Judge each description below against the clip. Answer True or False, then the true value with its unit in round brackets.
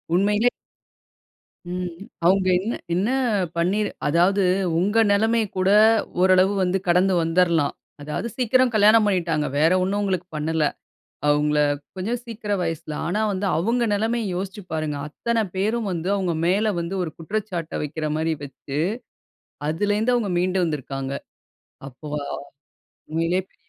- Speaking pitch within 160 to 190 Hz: True (185 Hz)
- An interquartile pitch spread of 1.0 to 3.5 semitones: False (4.2 semitones)